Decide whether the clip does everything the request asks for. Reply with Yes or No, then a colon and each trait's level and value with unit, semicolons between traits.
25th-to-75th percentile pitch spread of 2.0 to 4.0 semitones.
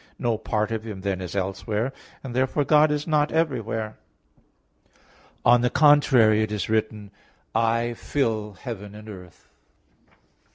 Yes: average, 3.6 semitones